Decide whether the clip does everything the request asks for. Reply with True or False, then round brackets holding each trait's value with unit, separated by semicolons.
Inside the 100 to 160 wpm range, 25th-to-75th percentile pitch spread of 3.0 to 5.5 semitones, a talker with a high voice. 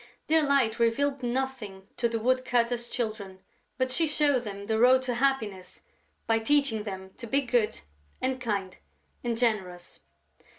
True (145 wpm; 3.5 semitones; 235 Hz)